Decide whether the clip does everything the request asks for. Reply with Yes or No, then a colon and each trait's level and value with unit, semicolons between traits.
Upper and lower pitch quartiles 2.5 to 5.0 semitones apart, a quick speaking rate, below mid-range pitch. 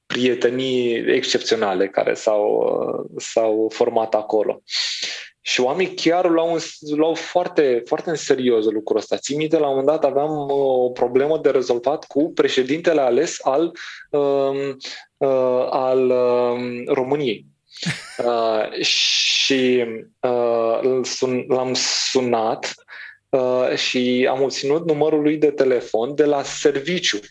No: average, 3.9 semitones; slow, 115 wpm; low, 130 Hz